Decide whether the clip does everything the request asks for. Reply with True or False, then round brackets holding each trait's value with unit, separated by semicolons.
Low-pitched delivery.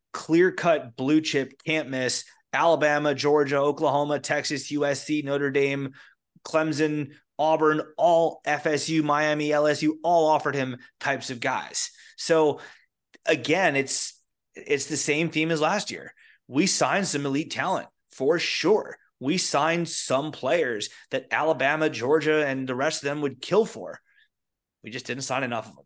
False (150 Hz)